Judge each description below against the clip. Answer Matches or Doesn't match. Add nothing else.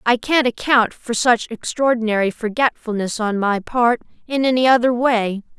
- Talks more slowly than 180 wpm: Matches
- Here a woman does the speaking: Matches